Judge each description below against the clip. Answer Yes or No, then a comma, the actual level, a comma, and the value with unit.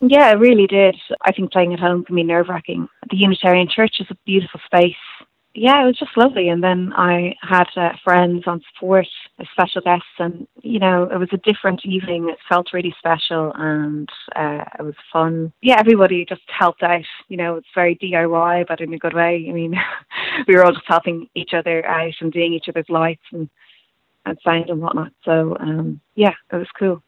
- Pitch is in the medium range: Yes, medium, 175 Hz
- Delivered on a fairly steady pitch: Yes, narrow, 2.2 semitones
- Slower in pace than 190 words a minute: No, fast, 205 wpm